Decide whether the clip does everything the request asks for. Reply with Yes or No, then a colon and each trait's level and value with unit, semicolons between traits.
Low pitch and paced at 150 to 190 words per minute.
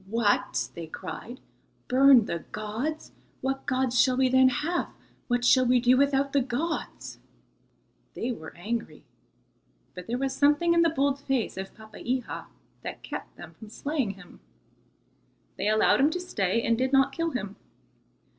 No: very high, 255 Hz; average, 155 wpm